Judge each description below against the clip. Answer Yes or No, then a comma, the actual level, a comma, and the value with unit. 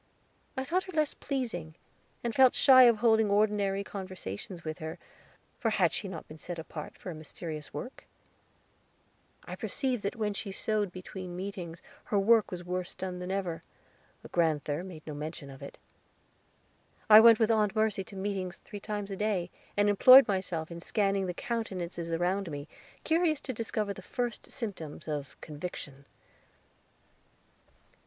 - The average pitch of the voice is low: No, high, 195 Hz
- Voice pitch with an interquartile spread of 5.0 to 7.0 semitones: No, average, 4.4 semitones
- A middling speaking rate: Yes, average, 160 wpm